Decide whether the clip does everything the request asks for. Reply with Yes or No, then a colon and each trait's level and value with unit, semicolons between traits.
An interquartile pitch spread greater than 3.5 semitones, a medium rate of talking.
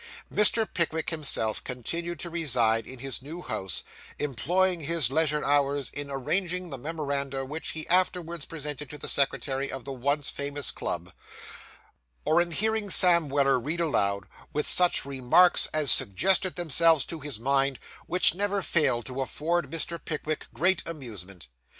Yes: average, 4.2 semitones; average, 150 wpm